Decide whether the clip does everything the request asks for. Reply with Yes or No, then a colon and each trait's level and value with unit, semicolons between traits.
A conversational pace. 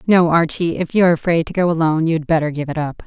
No: fast, 255 wpm